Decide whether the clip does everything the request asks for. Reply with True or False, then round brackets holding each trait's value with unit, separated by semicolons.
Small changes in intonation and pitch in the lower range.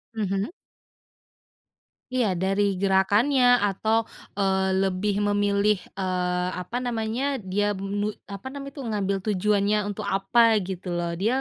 False (2.1 semitones; 200 Hz)